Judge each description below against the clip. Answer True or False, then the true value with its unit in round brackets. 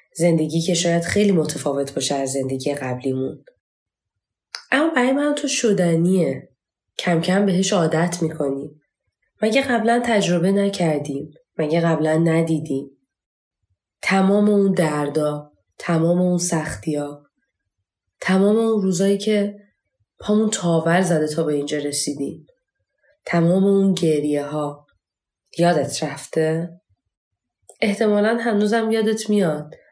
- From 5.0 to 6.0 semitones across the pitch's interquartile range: True (5.6 semitones)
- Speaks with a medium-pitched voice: True (165 Hz)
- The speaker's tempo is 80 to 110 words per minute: True (105 wpm)